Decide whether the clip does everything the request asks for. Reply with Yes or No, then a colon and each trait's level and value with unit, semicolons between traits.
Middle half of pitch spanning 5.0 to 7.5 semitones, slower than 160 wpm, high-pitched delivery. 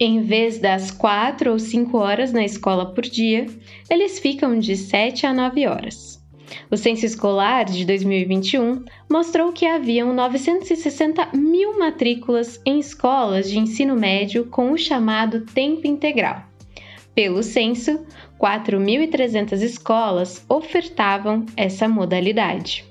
Yes: average, 5.3 semitones; slow, 120 wpm; high, 235 Hz